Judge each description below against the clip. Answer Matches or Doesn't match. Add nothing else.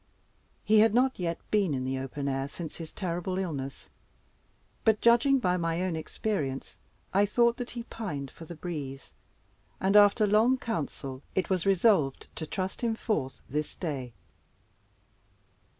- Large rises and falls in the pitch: Matches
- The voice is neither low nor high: Matches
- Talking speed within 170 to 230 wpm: Doesn't match